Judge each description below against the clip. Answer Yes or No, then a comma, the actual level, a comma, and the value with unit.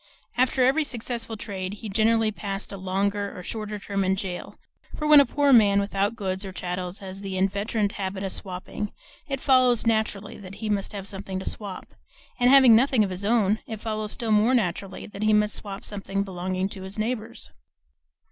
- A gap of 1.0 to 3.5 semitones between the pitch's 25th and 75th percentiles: Yes, average, 2.7 semitones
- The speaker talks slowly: No, average, 195 wpm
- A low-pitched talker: No, high, 205 Hz